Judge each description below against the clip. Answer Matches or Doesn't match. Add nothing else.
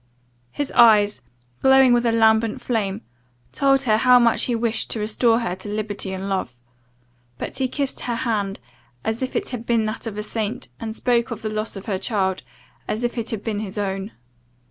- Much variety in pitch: Doesn't match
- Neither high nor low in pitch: Doesn't match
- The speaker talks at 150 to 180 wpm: Doesn't match